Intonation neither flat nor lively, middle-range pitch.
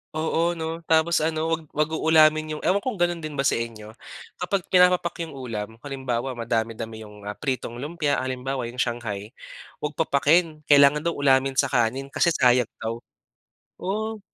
Yes: average, 5.0 semitones; medium, 145 Hz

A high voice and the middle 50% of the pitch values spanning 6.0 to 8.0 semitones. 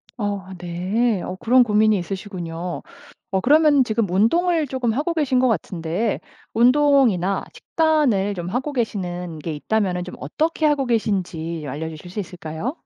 Yes: high, 210 Hz; wide, 6.4 semitones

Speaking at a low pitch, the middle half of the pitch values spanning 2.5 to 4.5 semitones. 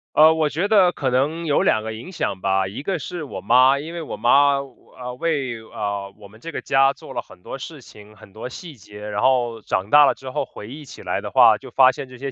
No: low, 130 Hz; wide, 5.6 semitones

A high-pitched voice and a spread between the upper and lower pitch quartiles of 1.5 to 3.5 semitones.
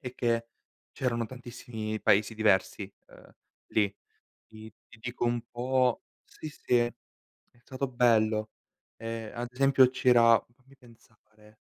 No: low, 120 Hz; narrow, 2.4 semitones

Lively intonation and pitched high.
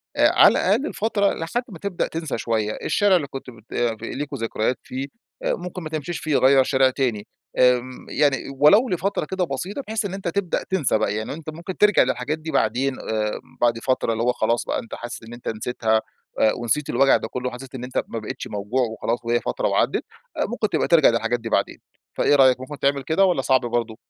No: wide, 5.9 semitones; low, 130 Hz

